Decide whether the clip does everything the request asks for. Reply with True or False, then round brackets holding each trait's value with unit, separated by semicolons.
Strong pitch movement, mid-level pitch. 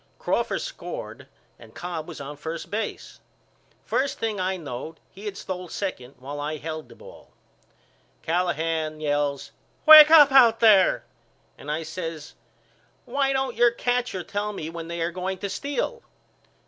True (6.3 semitones; 180 Hz)